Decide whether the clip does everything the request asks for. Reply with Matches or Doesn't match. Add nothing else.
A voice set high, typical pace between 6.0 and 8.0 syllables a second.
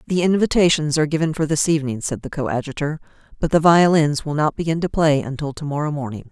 Doesn't match